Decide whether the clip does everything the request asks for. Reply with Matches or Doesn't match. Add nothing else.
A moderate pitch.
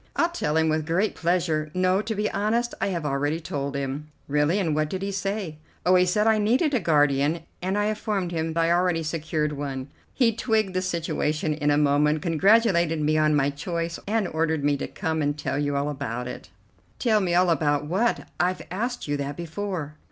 Matches